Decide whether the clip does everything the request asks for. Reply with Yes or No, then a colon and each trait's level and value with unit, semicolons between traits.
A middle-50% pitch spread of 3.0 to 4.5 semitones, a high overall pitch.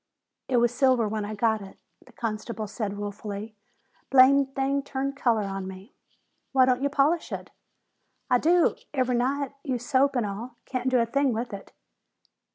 Yes: average, 4.1 semitones; high, 245 Hz